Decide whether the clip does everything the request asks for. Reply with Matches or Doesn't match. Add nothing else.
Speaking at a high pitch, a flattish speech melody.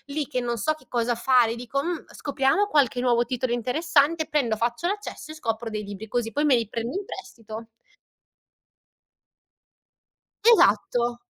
Doesn't match